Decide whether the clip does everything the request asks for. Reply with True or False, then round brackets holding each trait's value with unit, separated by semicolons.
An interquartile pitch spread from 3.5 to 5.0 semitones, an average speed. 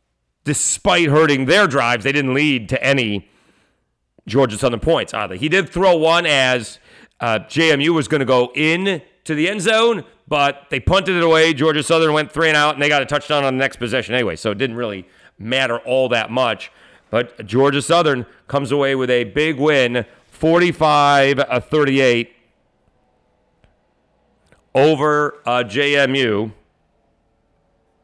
True (4.2 semitones; 150 wpm)